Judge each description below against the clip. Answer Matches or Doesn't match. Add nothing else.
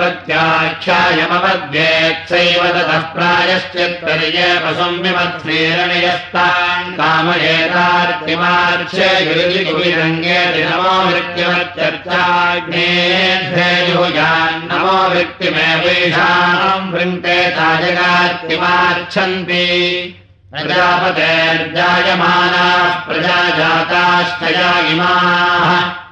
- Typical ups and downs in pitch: Doesn't match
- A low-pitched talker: Doesn't match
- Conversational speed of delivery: Doesn't match